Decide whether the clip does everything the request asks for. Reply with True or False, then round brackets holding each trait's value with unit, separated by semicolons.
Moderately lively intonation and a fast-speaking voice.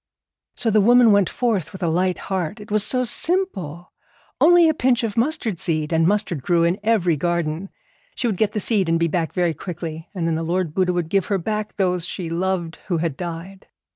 True (4.2 semitones; 215 wpm)